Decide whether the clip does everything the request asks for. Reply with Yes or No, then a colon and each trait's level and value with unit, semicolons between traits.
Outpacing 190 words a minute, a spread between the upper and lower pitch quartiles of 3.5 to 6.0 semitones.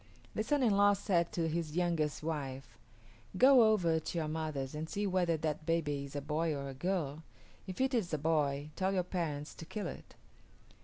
Yes: average, 200 wpm; average, 3.8 semitones